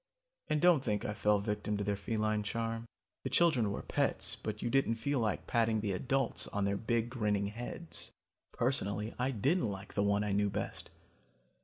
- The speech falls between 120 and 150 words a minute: No, average, 185 wpm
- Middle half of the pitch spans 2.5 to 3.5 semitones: Yes, average, 3.0 semitones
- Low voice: Yes, low, 110 Hz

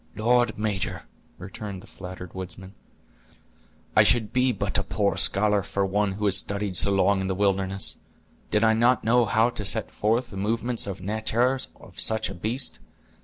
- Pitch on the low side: Yes, low, 105 Hz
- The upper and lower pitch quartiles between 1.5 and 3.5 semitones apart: Yes, average, 2.7 semitones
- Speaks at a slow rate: No, average, 175 wpm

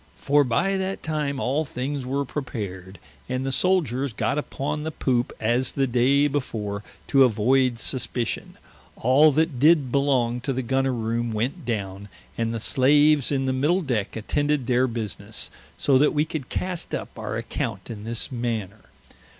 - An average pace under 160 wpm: No, average, 165 wpm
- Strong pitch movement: No, average, 3.7 semitones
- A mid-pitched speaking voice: No, low, 130 Hz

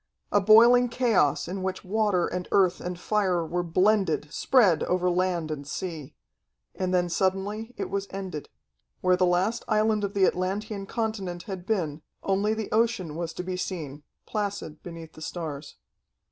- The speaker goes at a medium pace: Yes, average, 160 wpm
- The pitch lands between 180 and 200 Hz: Yes, medium, 185 Hz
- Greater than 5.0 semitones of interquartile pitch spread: No, average, 3.3 semitones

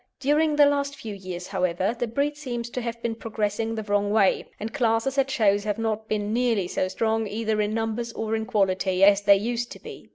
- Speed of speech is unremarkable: No, fast, 220 wpm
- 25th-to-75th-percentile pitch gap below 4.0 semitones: Yes, average, 2.7 semitones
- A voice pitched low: No, high, 225 Hz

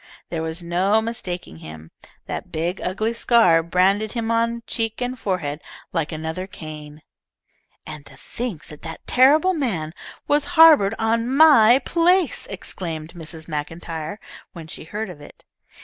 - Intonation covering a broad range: Yes, wide, 6.3 semitones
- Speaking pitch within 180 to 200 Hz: Yes, medium, 185 Hz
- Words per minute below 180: Yes, average, 145 wpm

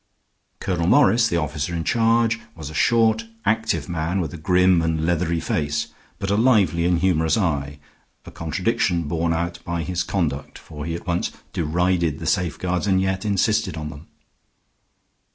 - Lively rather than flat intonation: No, average, 3.1 semitones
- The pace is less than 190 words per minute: Yes, average, 165 wpm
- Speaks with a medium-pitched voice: No, very low, 85 Hz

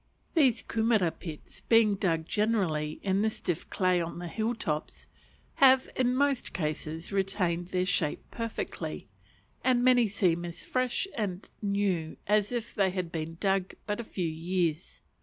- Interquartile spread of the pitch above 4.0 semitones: Yes, average, 4.8 semitones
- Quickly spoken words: No, average, 155 wpm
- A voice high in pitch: Yes, high, 195 Hz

